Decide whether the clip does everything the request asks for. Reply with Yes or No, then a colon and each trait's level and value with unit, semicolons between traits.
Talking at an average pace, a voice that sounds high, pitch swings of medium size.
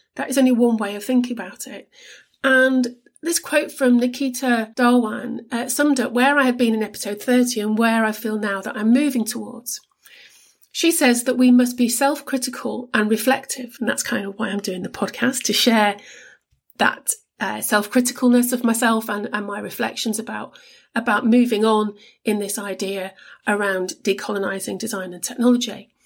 Yes: average, 175 wpm; high, 240 Hz; average, 3.1 semitones